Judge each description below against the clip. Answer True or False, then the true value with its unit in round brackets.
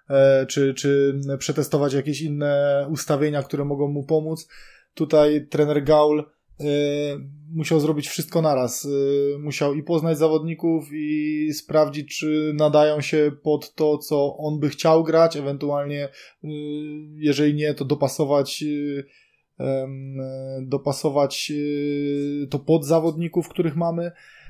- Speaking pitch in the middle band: True (150 Hz)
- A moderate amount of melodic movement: False (1.3 semitones)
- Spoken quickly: False (110 wpm)